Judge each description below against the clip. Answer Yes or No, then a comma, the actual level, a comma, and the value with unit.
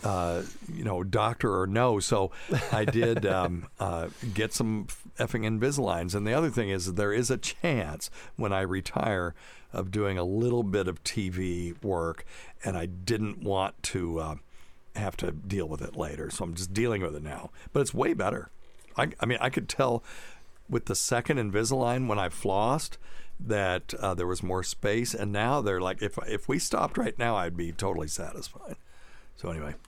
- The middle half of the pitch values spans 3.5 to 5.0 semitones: Yes, average, 4.4 semitones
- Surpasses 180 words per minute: Yes, average, 190 wpm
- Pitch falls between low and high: No, low, 100 Hz